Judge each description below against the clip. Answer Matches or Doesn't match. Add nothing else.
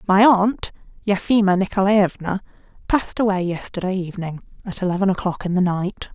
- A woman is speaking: Matches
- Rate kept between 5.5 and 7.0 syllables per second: Matches